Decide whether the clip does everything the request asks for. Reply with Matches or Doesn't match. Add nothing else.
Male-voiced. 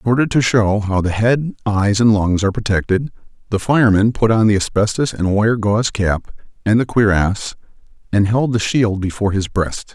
Matches